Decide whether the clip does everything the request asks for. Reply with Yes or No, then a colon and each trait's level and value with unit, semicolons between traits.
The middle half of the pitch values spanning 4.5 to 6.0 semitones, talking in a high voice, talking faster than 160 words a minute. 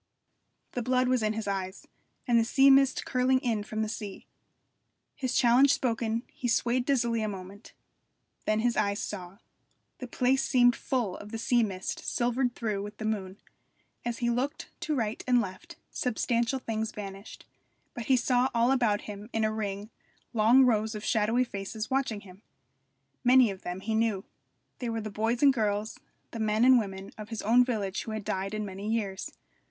No: average, 3.0 semitones; high, 225 Hz; average, 180 wpm